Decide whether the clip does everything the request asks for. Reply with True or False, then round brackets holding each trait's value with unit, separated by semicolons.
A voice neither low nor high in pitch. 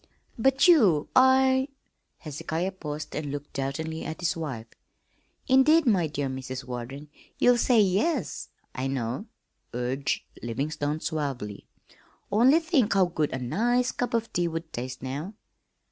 True (160 Hz)